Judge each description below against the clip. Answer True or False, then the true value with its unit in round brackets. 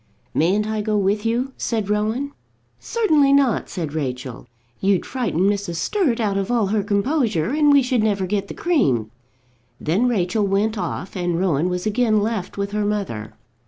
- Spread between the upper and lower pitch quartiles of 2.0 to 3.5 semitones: False (4.4 semitones)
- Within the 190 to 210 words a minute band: False (170 wpm)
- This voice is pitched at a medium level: False (205 Hz)